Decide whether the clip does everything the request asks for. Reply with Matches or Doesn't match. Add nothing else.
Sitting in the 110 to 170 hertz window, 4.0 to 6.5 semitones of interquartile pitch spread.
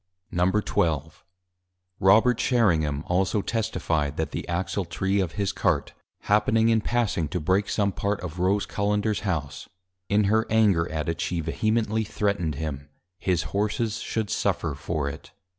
Doesn't match